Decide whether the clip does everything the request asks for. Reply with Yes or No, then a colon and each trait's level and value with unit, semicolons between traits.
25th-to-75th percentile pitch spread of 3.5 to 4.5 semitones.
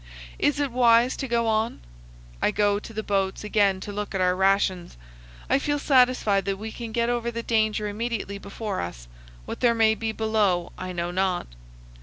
No: average, 3.1 semitones